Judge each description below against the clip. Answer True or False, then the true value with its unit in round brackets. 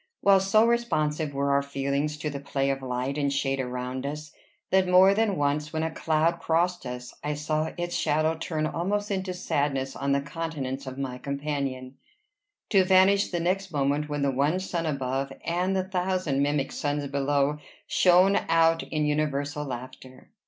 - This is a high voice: False (150 Hz)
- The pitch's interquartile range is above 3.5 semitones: True (4.0 semitones)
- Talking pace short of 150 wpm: False (175 wpm)